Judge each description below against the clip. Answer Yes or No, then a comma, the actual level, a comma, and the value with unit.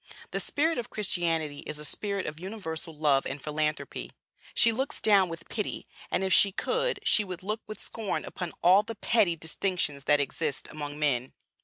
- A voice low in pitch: No, medium, 175 Hz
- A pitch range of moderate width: No, wide, 5.7 semitones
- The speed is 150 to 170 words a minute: No, average, 180 wpm